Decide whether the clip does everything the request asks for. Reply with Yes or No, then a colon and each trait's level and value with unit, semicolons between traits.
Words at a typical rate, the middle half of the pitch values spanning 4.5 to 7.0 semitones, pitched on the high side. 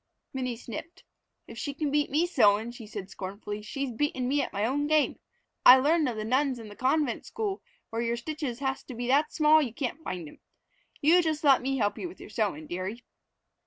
No: fast, 210 wpm; average, 5.0 semitones; very high, 260 Hz